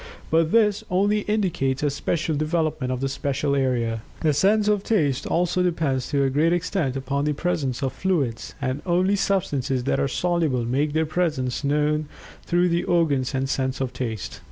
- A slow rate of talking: No, average, 180 wpm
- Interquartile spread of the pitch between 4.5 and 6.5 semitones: Yes, average, 4.8 semitones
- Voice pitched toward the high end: No, medium, 150 Hz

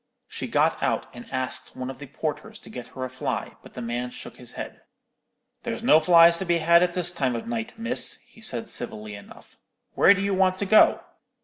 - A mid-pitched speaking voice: Yes, medium, 170 Hz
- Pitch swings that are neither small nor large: No, wide, 7.4 semitones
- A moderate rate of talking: No, fast, 220 wpm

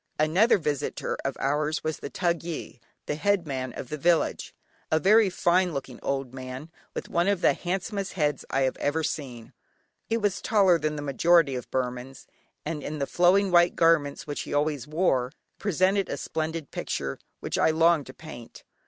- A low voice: No, medium, 155 Hz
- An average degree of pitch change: Yes, average, 4.2 semitones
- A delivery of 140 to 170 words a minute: No, average, 180 wpm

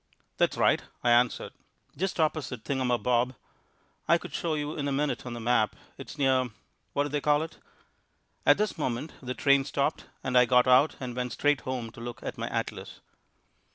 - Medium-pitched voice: No, low, 130 Hz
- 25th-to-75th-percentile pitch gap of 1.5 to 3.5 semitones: Yes, average, 3.0 semitones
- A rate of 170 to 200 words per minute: Yes, average, 190 wpm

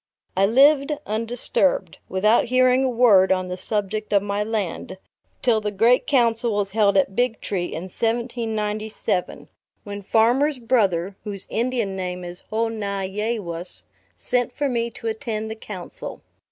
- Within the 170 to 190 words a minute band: No, average, 155 wpm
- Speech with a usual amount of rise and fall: Yes, average, 3.2 semitones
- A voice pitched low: No, high, 215 Hz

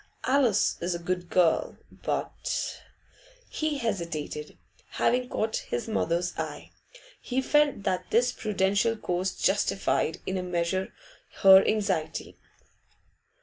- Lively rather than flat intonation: No, average, 4.8 semitones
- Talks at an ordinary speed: No, slow, 115 wpm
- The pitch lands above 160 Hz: Yes, high, 190 Hz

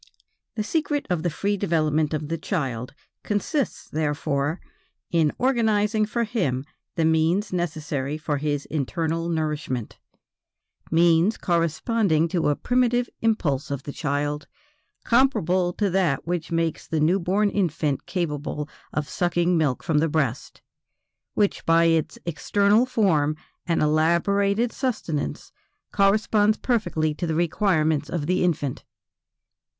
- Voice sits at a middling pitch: Yes, medium, 165 Hz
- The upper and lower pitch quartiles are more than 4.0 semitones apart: Yes, average, 4.9 semitones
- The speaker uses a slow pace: Yes, slow, 125 wpm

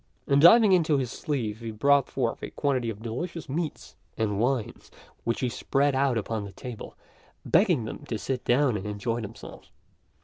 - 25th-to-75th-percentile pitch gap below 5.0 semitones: Yes, average, 4.1 semitones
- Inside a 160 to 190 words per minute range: Yes, average, 175 wpm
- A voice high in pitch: No, low, 125 Hz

